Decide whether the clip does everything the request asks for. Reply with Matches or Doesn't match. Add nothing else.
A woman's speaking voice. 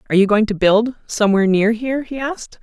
Matches